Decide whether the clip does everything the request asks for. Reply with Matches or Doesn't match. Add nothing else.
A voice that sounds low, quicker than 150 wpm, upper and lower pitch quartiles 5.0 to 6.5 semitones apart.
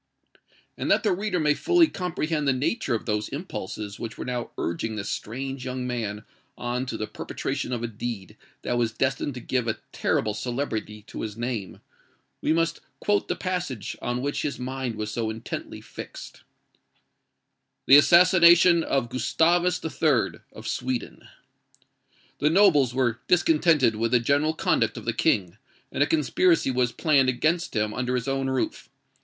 Matches